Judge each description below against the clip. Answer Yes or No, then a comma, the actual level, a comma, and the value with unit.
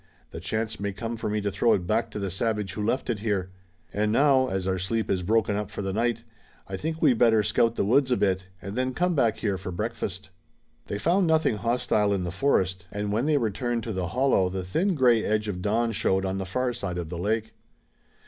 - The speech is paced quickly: Yes, fast, 235 wpm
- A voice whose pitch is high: No, low, 105 Hz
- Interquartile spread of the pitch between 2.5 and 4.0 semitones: Yes, average, 3.7 semitones